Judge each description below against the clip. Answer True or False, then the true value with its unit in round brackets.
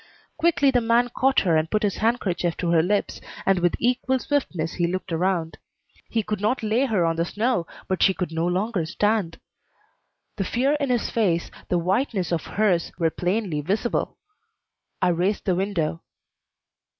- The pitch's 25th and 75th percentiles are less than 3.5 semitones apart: False (5.0 semitones)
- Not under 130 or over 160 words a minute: False (175 wpm)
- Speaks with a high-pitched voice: True (195 Hz)